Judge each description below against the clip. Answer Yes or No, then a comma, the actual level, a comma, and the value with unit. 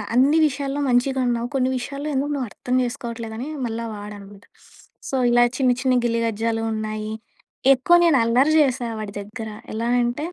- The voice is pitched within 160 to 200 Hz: No, high, 240 Hz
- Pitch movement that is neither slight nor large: Yes, average, 3.1 semitones